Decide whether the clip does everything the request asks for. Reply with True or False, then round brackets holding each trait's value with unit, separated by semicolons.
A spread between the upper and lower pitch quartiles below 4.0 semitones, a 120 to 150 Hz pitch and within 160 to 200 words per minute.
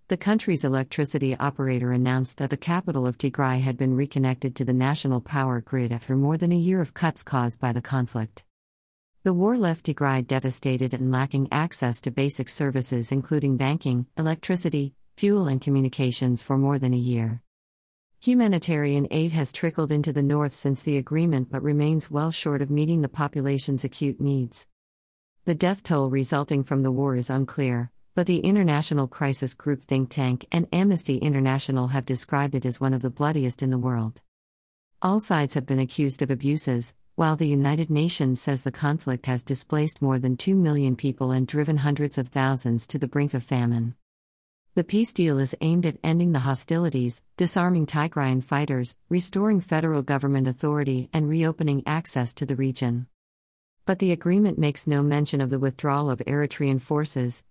True (2.9 semitones; 140 Hz; 175 wpm)